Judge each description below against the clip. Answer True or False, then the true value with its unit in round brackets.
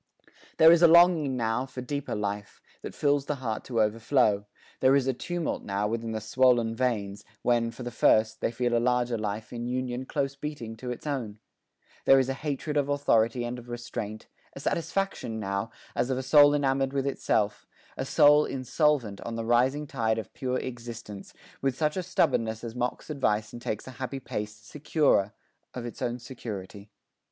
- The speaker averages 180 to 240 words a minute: True (185 wpm)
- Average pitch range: True (3.5 semitones)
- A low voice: True (125 Hz)